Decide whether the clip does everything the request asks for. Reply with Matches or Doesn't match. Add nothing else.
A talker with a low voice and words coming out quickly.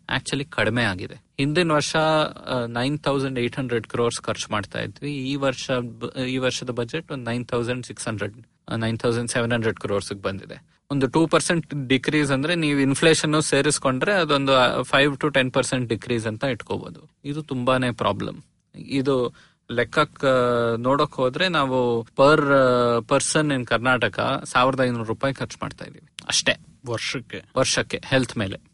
Matches